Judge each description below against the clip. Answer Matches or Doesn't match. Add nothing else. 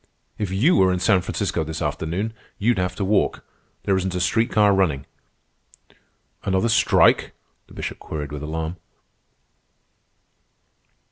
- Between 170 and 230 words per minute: Doesn't match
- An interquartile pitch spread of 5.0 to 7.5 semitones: Doesn't match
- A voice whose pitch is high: Doesn't match